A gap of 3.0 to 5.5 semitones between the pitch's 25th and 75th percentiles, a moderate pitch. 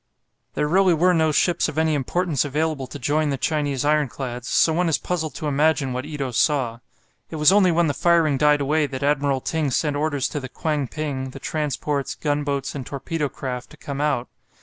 No: narrow, 2.5 semitones; medium, 145 Hz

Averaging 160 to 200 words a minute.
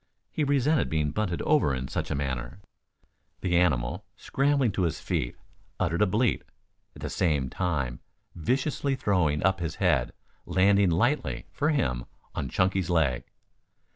No: average, 145 wpm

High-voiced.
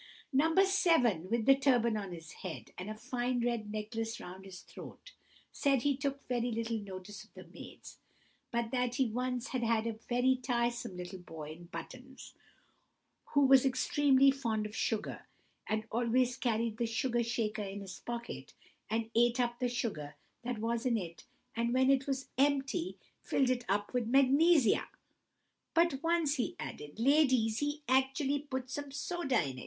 Yes: high, 240 Hz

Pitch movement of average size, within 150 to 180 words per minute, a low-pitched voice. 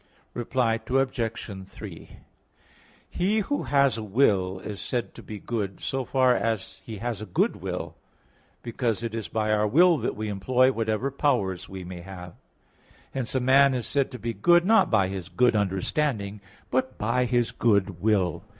Yes: average, 4.5 semitones; average, 170 wpm; low, 115 Hz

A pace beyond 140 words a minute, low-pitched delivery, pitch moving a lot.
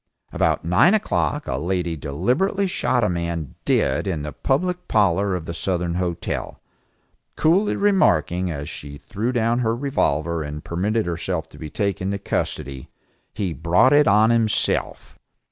Yes: average, 150 wpm; very low, 95 Hz; wide, 6.1 semitones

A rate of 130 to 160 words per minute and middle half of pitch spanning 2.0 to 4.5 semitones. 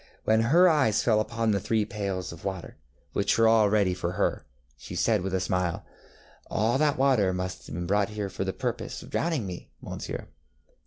No: average, 200 wpm; average, 3.5 semitones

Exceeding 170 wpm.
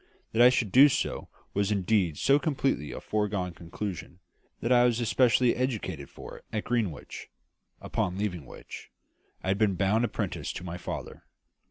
No: average, 165 wpm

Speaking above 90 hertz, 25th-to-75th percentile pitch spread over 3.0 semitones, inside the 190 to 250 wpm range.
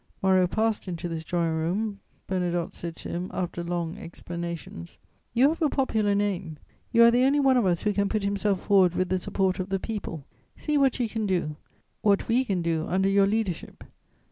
Yes: high, 190 Hz; average, 4.0 semitones; fast, 205 wpm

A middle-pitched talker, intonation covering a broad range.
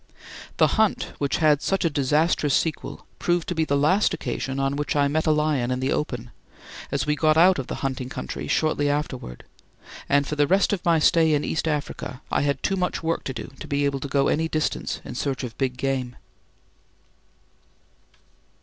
No: medium, 145 Hz; average, 2.8 semitones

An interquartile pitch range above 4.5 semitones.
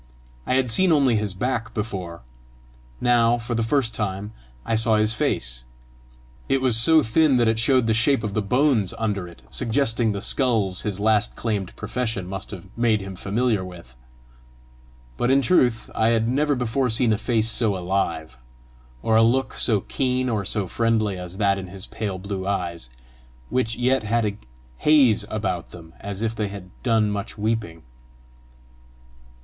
No: average, 3.5 semitones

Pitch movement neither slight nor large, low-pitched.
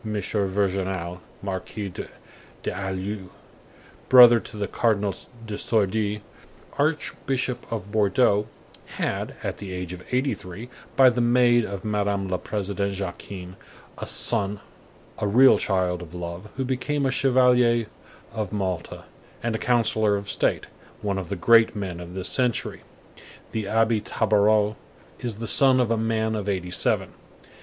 Yes: average, 3.5 semitones; low, 105 Hz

